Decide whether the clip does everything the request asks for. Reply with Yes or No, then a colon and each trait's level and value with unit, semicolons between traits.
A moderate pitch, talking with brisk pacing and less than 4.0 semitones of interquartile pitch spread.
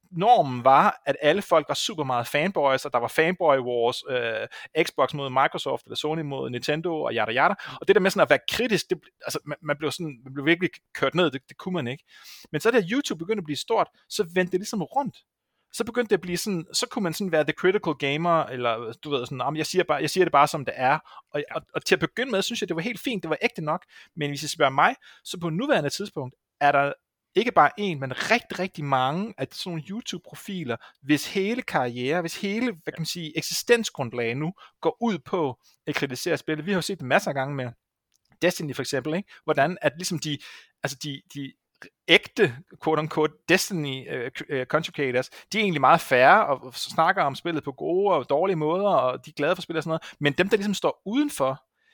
No: medium, 160 Hz; fast, 235 wpm; average, 5.2 semitones